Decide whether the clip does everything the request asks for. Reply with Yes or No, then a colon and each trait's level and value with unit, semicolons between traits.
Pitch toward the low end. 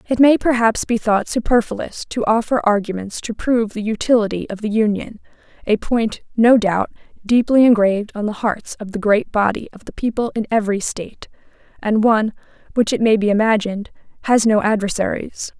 No: high, 220 Hz